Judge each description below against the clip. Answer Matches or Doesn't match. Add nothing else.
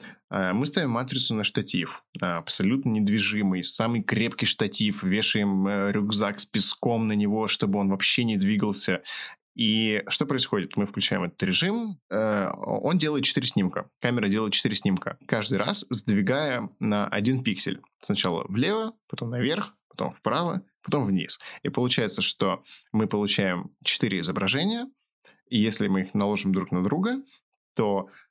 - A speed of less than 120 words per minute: Doesn't match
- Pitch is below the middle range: Matches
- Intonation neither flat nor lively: Doesn't match